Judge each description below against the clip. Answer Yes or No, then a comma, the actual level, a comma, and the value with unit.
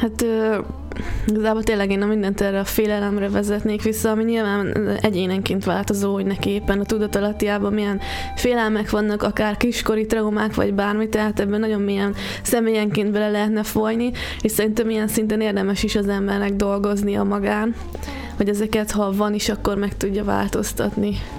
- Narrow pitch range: Yes, narrow, 1.4 semitones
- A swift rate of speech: Yes, fast, 160 wpm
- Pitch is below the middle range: No, high, 210 Hz